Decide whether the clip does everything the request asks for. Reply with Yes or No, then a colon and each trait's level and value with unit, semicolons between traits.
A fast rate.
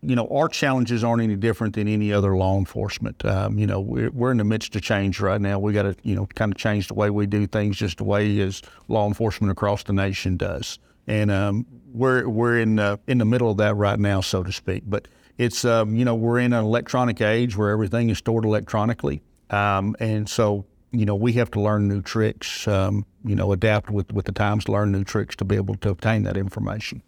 Yes: fast, 235 wpm